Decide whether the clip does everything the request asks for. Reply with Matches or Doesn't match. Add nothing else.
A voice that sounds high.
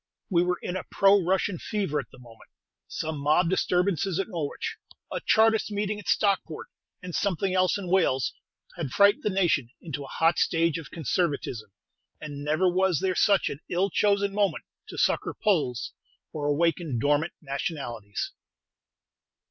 Doesn't match